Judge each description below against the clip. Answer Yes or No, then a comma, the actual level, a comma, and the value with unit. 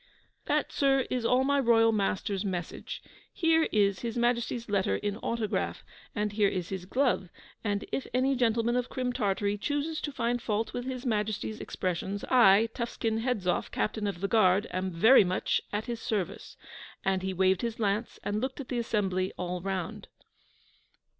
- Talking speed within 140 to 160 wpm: No, average, 170 wpm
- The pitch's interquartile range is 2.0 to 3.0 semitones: No, average, 4.0 semitones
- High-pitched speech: Yes, high, 215 Hz